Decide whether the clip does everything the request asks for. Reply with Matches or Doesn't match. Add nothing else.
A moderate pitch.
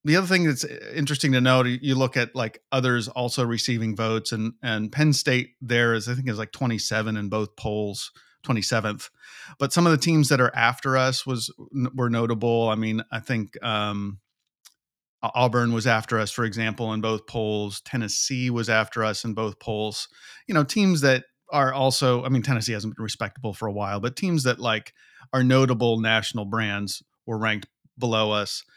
Doesn't match